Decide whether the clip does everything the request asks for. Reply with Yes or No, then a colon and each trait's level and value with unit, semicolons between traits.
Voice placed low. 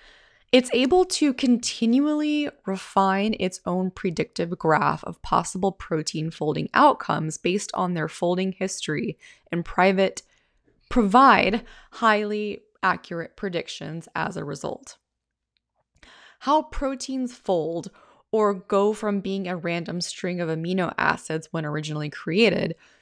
No: high, 190 Hz